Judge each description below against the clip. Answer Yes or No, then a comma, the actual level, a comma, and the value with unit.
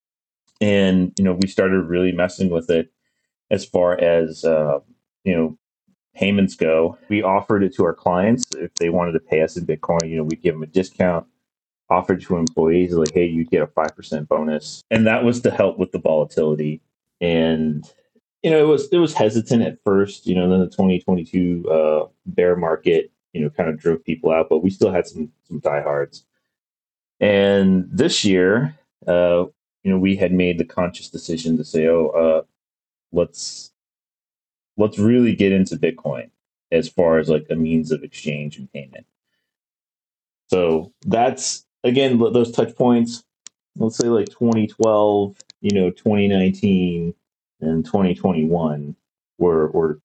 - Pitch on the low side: Yes, very low, 90 Hz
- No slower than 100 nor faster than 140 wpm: No, average, 165 wpm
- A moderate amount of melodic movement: Yes, average, 3.8 semitones